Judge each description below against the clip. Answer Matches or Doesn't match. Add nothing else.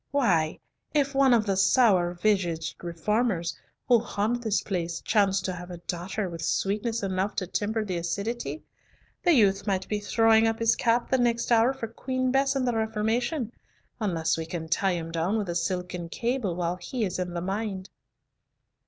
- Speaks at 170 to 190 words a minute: Matches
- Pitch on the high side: Matches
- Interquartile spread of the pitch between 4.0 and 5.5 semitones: Matches